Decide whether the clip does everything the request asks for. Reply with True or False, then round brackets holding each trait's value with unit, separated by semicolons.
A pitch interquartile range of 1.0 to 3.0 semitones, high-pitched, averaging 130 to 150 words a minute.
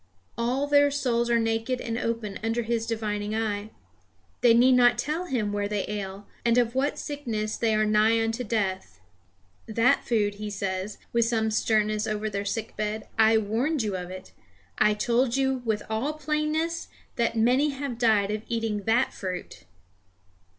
False (2.7 semitones; 225 Hz; 170 wpm)